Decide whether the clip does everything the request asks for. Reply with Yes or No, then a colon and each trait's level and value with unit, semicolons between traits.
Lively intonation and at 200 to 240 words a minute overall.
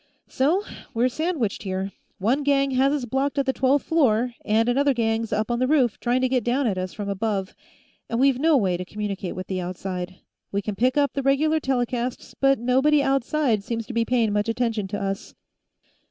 No: average, 4.7 semitones; fast, 205 wpm